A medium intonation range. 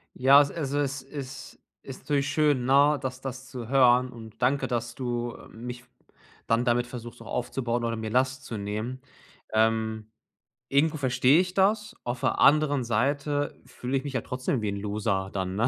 Yes: average, 3.0 semitones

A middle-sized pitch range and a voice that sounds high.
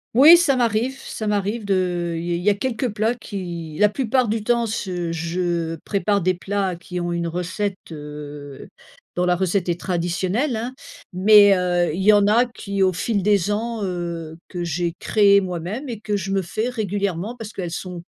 Yes: average, 3.7 semitones; high, 195 Hz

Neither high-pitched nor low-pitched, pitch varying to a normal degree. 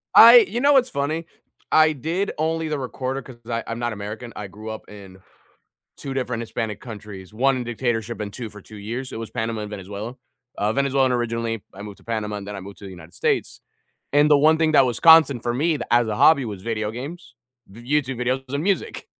No: low, 120 Hz; average, 4.8 semitones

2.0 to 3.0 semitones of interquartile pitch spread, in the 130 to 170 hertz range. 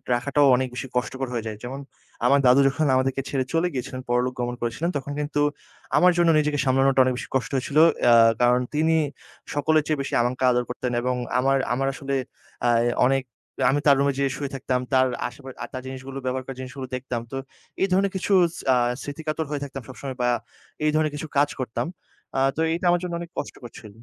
Yes: narrow, 2.4 semitones; low, 135 Hz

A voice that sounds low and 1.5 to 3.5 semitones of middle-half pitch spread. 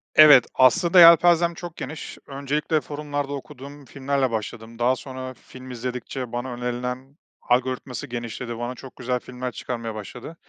Yes: low, 130 Hz; average, 2.8 semitones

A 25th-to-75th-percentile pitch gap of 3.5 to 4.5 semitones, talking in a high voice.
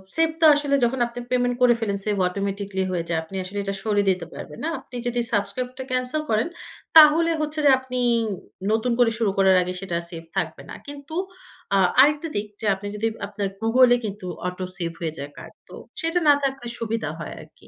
No: average, 5.1 semitones; high, 225 Hz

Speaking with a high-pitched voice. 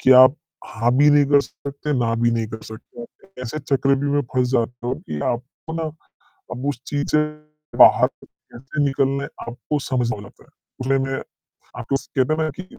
No: low, 135 Hz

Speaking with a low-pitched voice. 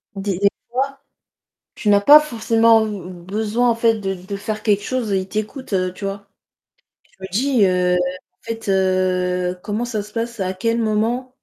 No: high, 210 Hz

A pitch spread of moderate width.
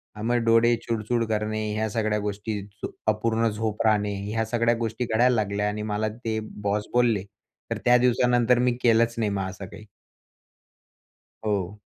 No: narrow, 1.9 semitones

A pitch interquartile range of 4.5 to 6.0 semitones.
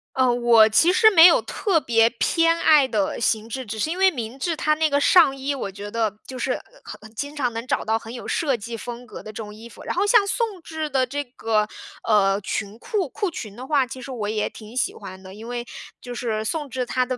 Yes: wide, 5.5 semitones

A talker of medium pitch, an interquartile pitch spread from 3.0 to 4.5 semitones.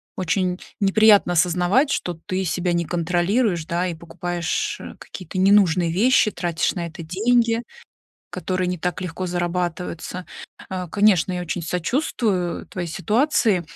No: medium, 180 Hz; narrow, 2.6 semitones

